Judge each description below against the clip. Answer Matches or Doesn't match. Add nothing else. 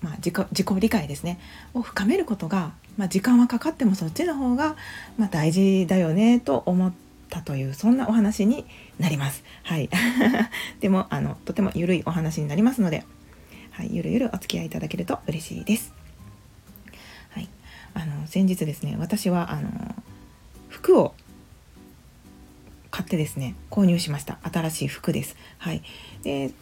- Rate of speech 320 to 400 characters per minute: Doesn't match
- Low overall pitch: Doesn't match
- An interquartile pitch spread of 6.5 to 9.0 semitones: Doesn't match